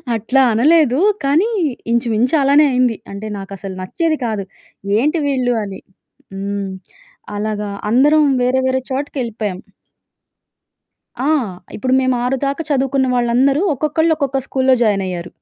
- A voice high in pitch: Yes, very high, 255 Hz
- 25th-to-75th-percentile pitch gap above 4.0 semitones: Yes, average, 4.5 semitones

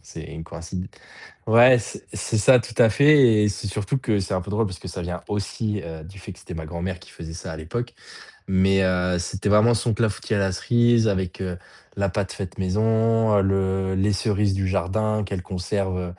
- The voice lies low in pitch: Yes, very low, 95 Hz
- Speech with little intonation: No, average, 3.0 semitones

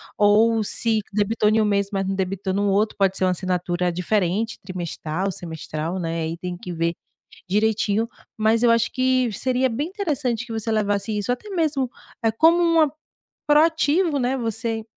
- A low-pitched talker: No, high, 215 Hz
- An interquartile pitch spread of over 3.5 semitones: Yes, average, 4.7 semitones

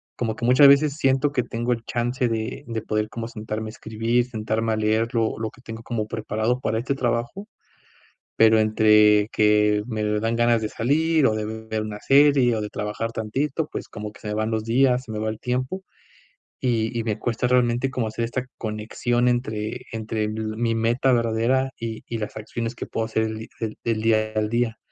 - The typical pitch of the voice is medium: No, low, 115 Hz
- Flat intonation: Yes, narrow, 2.1 semitones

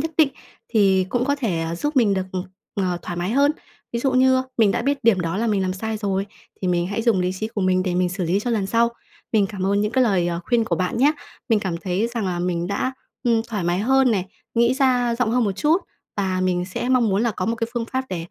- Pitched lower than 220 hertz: Yes, high, 210 Hz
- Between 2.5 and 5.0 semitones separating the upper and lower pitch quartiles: Yes, average, 4.5 semitones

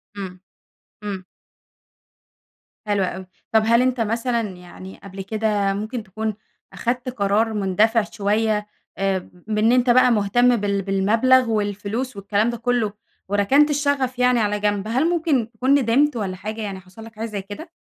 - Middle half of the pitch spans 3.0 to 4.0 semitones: Yes, average, 3.3 semitones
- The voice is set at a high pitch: Yes, high, 220 Hz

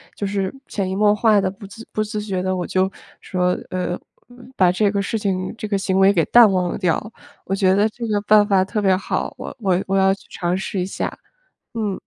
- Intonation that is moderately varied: No, narrow, 2.0 semitones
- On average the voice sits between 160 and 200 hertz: Yes, high, 195 Hz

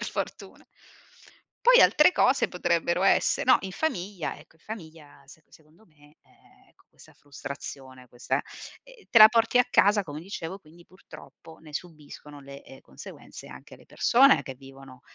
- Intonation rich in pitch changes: Yes, wide, 6.3 semitones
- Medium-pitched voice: Yes, medium, 165 Hz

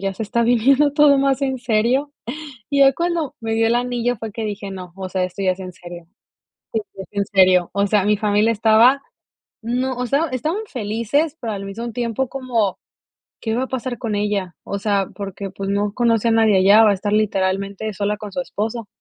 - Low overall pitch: No, high, 220 Hz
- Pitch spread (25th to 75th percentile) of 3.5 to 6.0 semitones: Yes, average, 3.8 semitones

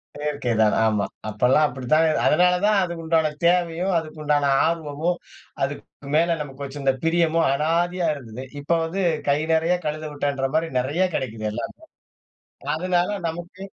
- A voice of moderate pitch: Yes, medium, 155 Hz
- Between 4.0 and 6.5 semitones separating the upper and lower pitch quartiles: No, average, 3.4 semitones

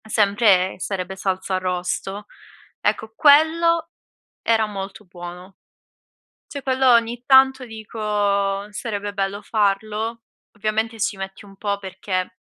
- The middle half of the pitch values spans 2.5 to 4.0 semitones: Yes, average, 2.9 semitones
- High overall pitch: Yes, high, 205 Hz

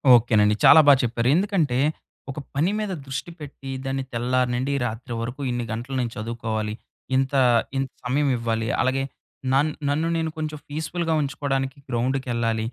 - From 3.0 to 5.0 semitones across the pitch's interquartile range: Yes, average, 3.5 semitones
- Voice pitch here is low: Yes, low, 130 Hz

